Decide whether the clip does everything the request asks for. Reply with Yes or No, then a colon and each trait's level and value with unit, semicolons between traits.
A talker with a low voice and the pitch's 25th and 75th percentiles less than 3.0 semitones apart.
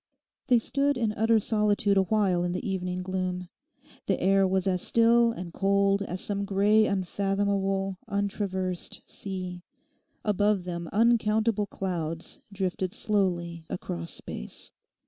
No: high, 195 Hz; narrow, 2.5 semitones